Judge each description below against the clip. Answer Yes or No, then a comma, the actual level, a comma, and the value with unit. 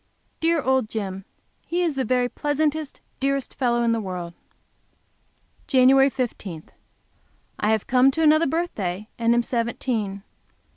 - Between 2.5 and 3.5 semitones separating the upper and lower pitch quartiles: No, average, 4.4 semitones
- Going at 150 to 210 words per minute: No, slow, 135 wpm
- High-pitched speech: Yes, very high, 250 Hz